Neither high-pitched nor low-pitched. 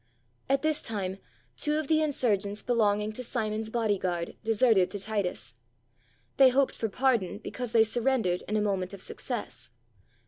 No: high, 220 Hz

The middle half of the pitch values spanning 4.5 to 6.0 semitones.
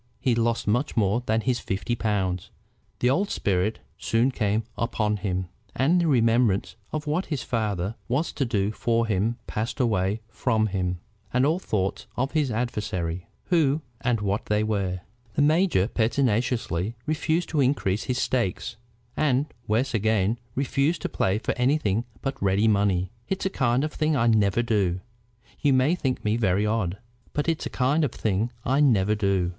Yes: average, 4.8 semitones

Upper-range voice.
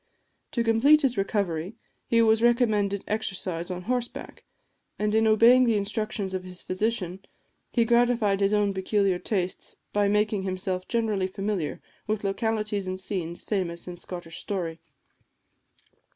Yes: high, 205 Hz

